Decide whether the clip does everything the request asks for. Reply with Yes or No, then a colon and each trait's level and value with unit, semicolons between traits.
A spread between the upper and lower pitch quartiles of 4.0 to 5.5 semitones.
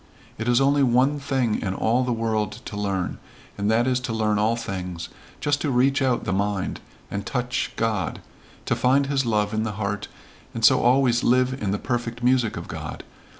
No: average, 3.5 semitones